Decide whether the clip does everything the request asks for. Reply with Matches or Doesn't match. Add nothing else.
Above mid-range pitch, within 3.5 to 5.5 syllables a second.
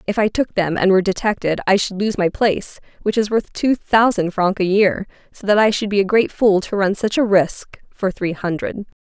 Matches